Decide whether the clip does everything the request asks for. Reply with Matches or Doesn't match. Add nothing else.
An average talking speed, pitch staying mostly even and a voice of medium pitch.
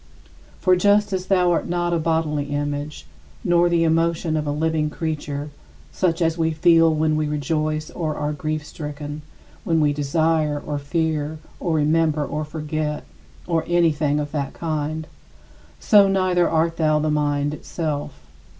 Matches